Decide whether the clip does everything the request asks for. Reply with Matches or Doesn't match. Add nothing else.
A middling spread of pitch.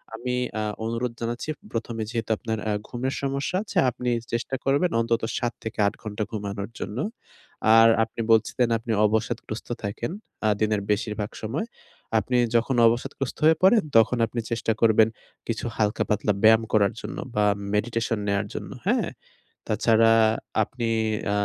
Doesn't match